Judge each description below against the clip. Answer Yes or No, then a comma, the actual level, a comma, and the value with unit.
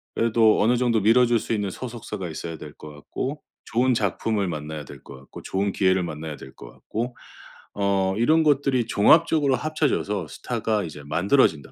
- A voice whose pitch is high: No, low, 105 Hz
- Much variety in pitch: Yes, wide, 6.4 semitones